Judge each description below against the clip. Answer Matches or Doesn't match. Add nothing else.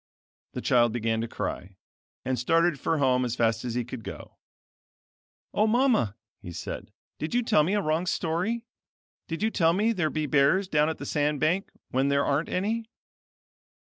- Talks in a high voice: Doesn't match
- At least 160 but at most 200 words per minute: Matches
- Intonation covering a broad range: Matches